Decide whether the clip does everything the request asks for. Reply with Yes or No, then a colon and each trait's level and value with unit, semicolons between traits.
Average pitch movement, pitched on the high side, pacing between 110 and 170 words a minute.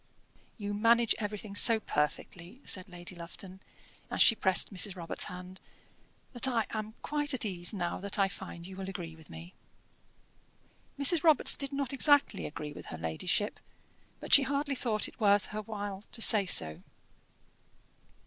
Yes: average, 4.5 semitones; high, 205 Hz; average, 160 wpm